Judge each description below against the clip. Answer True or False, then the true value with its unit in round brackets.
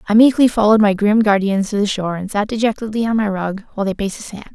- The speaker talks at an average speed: False (265 wpm)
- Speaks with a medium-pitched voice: False (210 Hz)